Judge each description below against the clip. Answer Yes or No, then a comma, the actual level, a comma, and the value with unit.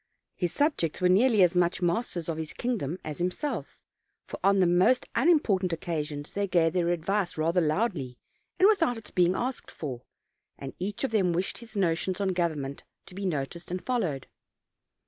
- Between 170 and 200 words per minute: Yes, average, 180 wpm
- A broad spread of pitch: No, average, 3.8 semitones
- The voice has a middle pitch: Yes, medium, 180 Hz